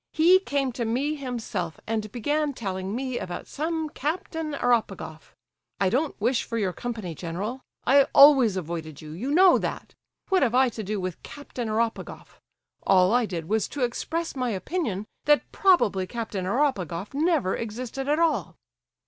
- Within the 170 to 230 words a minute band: No, average, 155 wpm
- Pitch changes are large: Yes, wide, 6.7 semitones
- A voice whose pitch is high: Yes, high, 240 Hz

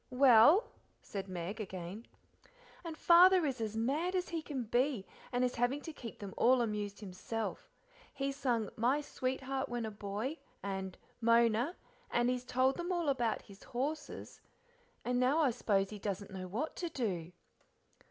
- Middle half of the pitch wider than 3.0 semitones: Yes, average, 5.1 semitones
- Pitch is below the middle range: No, high, 245 Hz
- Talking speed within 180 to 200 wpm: No, average, 160 wpm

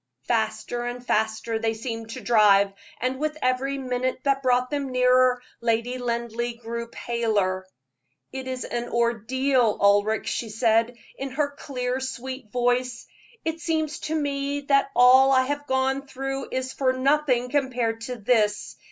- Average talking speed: Yes, average, 150 wpm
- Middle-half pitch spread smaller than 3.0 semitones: Yes, narrow, 2.6 semitones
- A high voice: Yes, very high, 250 Hz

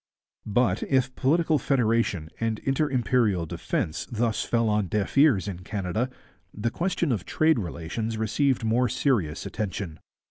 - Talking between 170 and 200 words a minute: No, average, 140 wpm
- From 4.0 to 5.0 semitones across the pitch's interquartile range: Yes, average, 4.7 semitones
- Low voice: Yes, low, 115 Hz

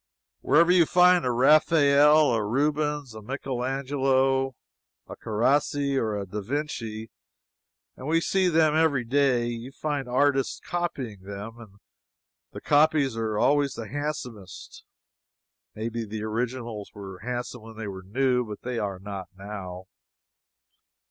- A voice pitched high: No, low, 125 Hz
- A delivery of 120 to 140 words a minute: Yes, slow, 135 wpm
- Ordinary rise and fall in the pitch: Yes, average, 4.9 semitones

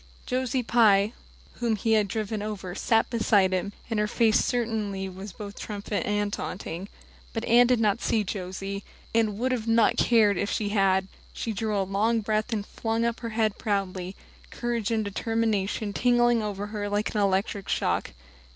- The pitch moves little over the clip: Yes, narrow, 2.2 semitones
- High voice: Yes, high, 210 Hz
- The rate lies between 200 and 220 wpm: No, average, 175 wpm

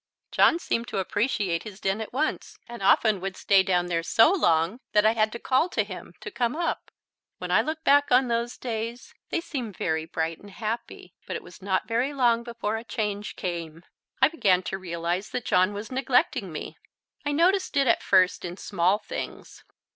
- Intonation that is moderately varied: Yes, average, 4.9 semitones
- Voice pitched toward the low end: No, high, 215 Hz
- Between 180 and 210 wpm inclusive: Yes, average, 200 wpm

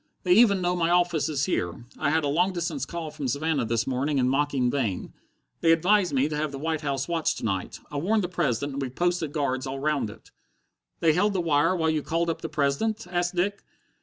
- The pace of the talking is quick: Yes, fast, 230 wpm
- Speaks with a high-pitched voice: No, medium, 155 Hz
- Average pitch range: Yes, average, 4.1 semitones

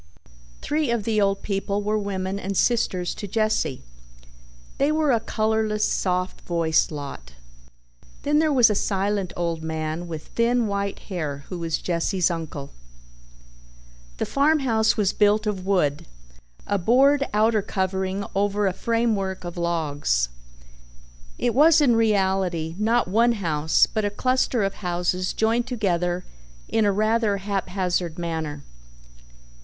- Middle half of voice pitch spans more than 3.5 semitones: Yes, average, 4.2 semitones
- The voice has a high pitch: Yes, high, 200 Hz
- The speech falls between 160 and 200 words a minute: No, slow, 135 wpm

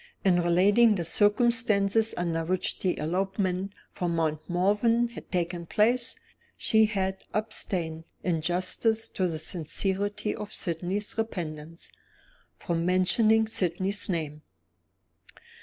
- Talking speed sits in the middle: No, slow, 110 wpm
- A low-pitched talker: No, medium, 185 Hz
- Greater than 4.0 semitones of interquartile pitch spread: No, average, 3.7 semitones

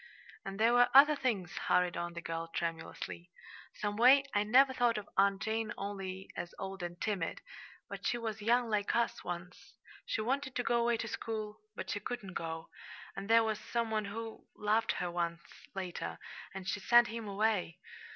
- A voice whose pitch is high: Yes, high, 210 Hz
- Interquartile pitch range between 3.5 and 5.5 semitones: Yes, average, 4.2 semitones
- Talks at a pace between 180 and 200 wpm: Yes, average, 185 wpm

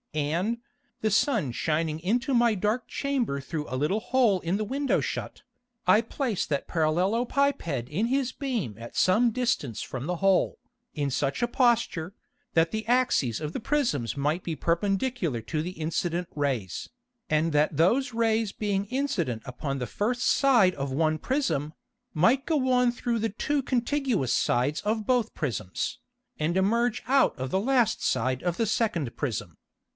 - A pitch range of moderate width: No, wide, 8.1 semitones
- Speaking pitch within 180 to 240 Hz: Yes, high, 190 Hz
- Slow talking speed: No, average, 160 wpm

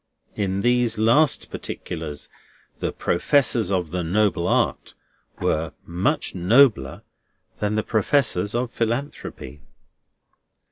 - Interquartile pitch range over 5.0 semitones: Yes, wide, 5.4 semitones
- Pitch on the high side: No, low, 105 Hz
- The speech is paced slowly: Yes, slow, 100 wpm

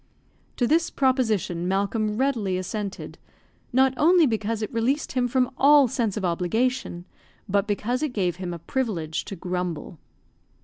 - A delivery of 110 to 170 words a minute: Yes, average, 145 wpm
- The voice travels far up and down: Yes, wide, 5.7 semitones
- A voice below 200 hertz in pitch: No, high, 220 Hz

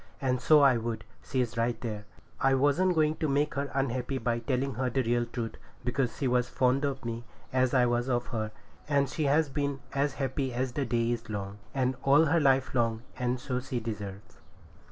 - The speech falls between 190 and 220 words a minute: Yes, fast, 205 wpm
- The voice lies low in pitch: Yes, low, 130 Hz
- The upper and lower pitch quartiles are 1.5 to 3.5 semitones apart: Yes, average, 2.8 semitones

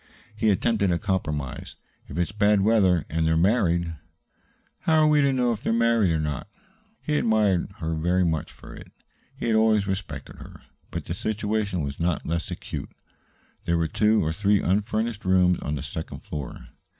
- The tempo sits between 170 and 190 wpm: Yes, average, 185 wpm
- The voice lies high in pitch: No, very low, 95 Hz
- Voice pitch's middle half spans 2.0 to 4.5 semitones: No, average, 4.9 semitones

